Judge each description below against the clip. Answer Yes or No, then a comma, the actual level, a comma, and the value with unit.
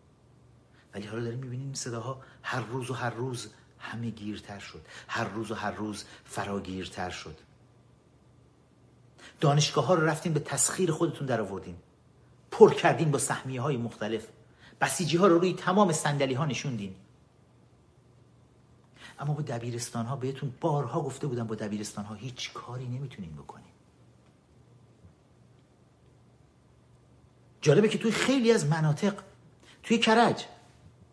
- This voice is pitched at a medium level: No, low, 130 Hz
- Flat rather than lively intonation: No, average, 5.0 semitones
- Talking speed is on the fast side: No, average, 130 wpm